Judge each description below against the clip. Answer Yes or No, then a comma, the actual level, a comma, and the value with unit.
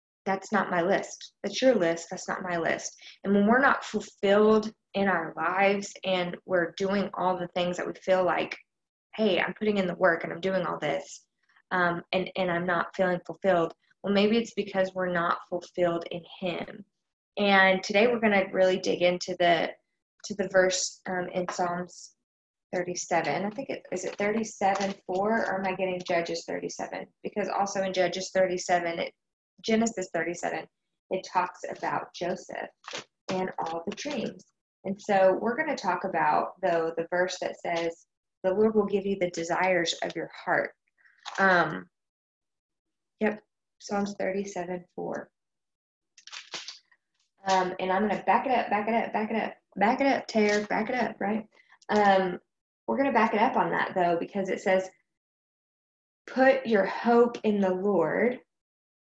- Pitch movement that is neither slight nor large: No, narrow, 2.3 semitones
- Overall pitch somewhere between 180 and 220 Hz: Yes, high, 190 Hz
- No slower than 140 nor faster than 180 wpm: Yes, average, 175 wpm